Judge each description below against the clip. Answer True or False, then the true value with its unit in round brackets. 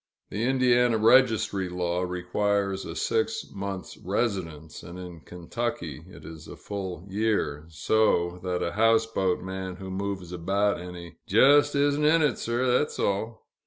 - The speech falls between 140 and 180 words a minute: True (145 wpm)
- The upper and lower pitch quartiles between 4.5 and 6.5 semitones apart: False (4.1 semitones)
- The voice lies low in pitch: True (100 Hz)